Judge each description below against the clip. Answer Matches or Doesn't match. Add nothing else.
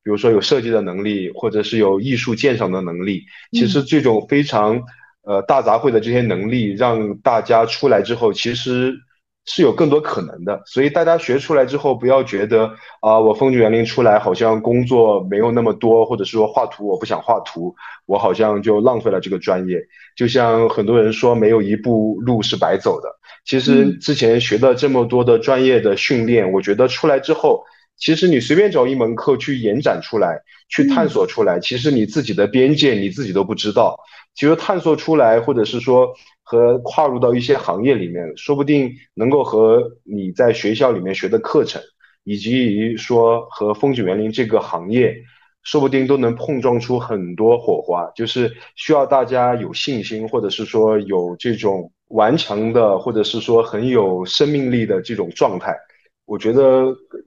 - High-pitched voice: Doesn't match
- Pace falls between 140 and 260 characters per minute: Doesn't match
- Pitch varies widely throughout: Doesn't match